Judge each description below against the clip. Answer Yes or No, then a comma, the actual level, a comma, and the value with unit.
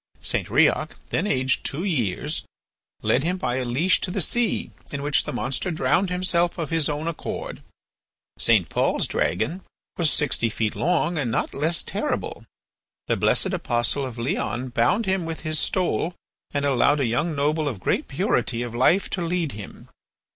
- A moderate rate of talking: Yes, average, 170 wpm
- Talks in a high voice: No, medium, 150 Hz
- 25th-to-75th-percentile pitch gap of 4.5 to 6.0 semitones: Yes, wide, 5.4 semitones